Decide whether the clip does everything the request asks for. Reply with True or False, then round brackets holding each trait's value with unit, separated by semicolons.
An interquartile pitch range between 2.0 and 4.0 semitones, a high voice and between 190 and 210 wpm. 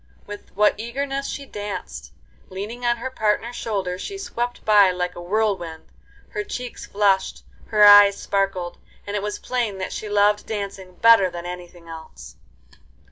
False (3.6 semitones; 205 Hz; 155 wpm)